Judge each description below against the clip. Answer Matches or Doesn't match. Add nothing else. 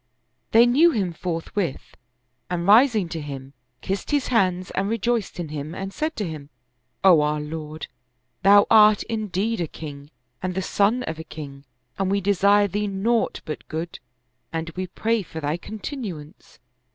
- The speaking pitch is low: Doesn't match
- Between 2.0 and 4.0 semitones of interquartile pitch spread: Doesn't match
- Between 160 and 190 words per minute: Matches